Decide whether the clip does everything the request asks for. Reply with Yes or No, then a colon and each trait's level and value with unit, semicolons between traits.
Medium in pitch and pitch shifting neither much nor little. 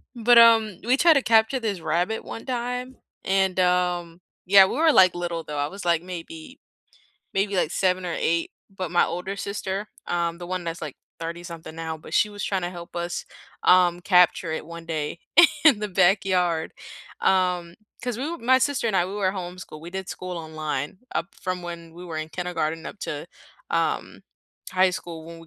Yes: medium, 180 Hz; average, 3.0 semitones